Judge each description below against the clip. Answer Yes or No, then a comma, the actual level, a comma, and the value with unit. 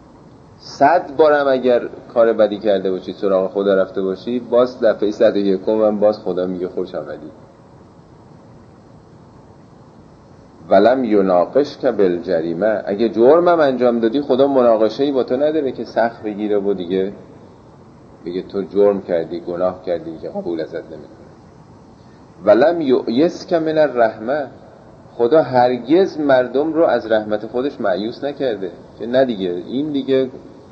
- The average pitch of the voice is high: No, low, 115 Hz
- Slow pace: No, average, 135 wpm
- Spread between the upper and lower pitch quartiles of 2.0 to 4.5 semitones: No, average, 4.9 semitones